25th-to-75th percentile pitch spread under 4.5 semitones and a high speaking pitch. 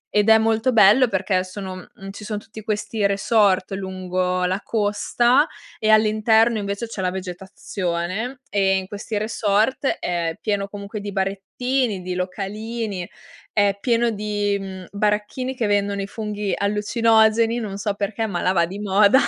Yes: narrow, 2.4 semitones; high, 205 Hz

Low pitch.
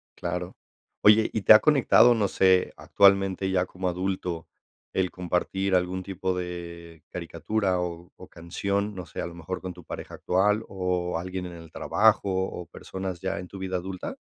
Yes: very low, 95 Hz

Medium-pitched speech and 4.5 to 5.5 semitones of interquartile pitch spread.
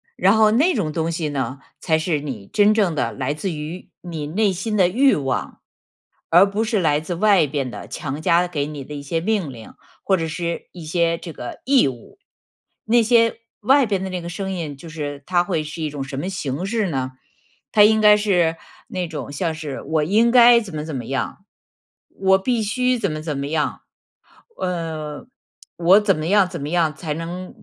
Yes: medium, 170 Hz; average, 5.1 semitones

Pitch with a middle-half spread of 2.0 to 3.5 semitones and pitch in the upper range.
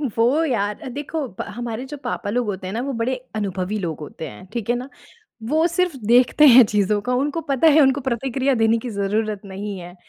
No: average, 4.6 semitones; high, 235 Hz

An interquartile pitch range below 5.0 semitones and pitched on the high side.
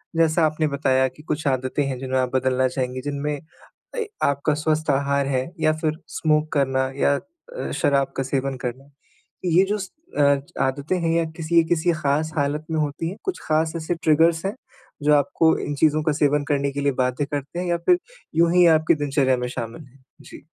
No: average, 3.0 semitones; medium, 145 Hz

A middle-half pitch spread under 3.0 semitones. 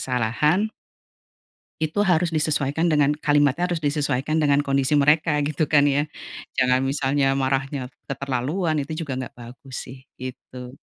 Yes: narrow, 2.6 semitones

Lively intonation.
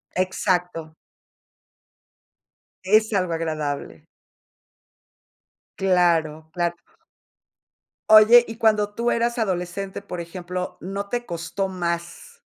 No: average, 3.8 semitones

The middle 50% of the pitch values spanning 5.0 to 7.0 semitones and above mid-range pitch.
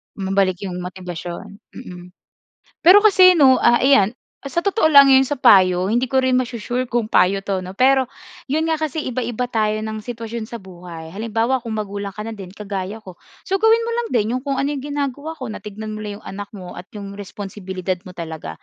Yes: wide, 5.4 semitones; high, 220 Hz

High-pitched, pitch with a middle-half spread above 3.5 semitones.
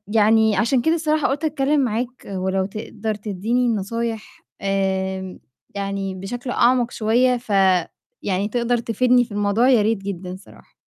Yes: high, 220 Hz; average, 3.9 semitones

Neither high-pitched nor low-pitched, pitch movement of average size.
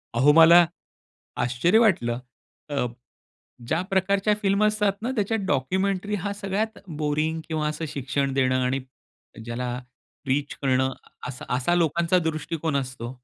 No: medium, 155 Hz; wide, 6.6 semitones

